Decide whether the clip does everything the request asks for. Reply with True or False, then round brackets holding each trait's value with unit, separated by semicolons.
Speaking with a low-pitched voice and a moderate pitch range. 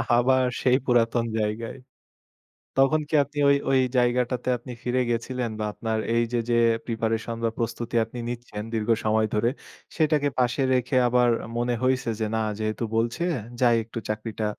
False (120 Hz; 2.0 semitones)